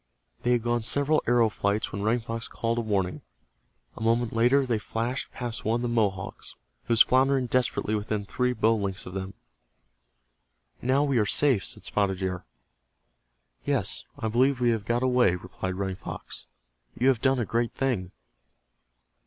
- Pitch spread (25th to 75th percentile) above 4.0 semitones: No, average, 3.4 semitones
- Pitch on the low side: Yes, low, 115 Hz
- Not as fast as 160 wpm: No, average, 170 wpm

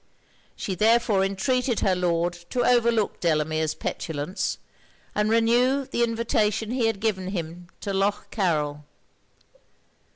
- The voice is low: No, high, 200 Hz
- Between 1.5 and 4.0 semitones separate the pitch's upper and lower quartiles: No, average, 4.8 semitones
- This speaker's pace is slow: Yes, slow, 120 wpm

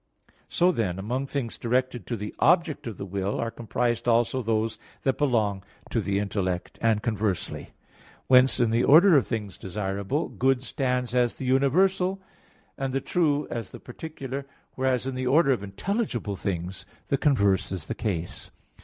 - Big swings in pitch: No, average, 4.8 semitones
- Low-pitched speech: Yes, low, 120 Hz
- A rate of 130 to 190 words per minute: Yes, average, 165 wpm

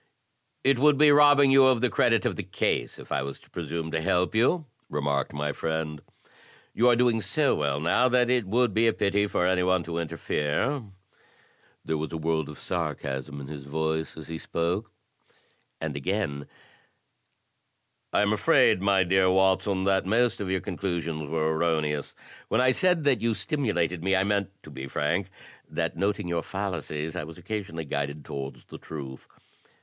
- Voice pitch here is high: No, very low, 90 Hz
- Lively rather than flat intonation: Yes, wide, 6.0 semitones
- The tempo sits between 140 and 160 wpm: No, average, 185 wpm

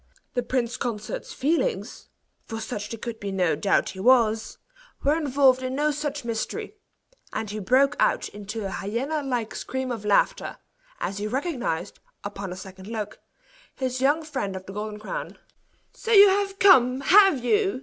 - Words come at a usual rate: Yes, average, 170 wpm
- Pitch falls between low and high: No, high, 245 Hz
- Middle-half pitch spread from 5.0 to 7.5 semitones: Yes, wide, 5.6 semitones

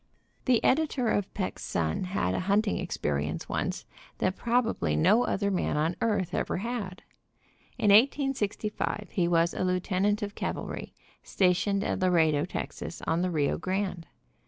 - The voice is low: No, high, 190 Hz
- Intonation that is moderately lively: Yes, average, 3.6 semitones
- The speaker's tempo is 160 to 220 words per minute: No, average, 145 wpm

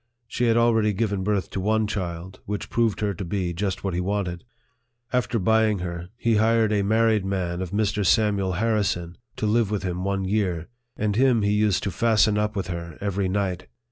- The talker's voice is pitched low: Yes, low, 100 Hz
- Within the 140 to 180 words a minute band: No, average, 200 wpm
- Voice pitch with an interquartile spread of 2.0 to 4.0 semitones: Yes, average, 2.8 semitones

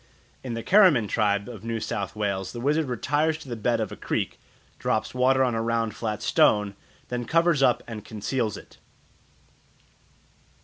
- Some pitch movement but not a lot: Yes, average, 3.7 semitones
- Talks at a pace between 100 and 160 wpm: No, average, 170 wpm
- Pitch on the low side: Yes, low, 115 Hz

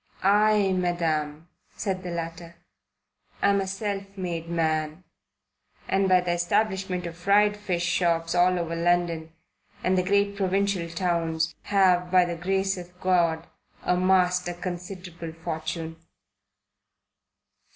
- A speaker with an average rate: No, slow, 120 wpm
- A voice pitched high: No, medium, 180 Hz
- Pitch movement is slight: Yes, narrow, 2.2 semitones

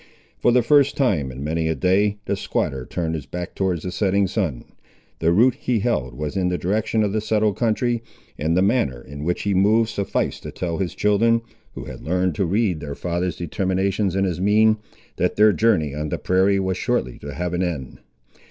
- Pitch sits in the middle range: No, very low, 95 Hz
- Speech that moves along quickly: Yes, fast, 210 wpm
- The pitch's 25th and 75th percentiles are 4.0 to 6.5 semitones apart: Yes, average, 4.4 semitones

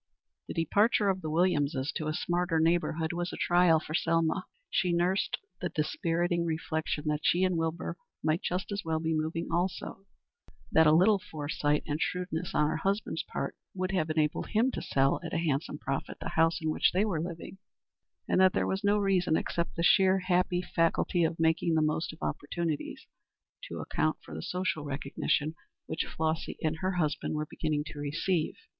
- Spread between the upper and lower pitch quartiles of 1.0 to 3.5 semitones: Yes, narrow, 2.6 semitones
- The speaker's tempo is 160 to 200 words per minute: Yes, average, 185 wpm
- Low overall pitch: No, medium, 165 Hz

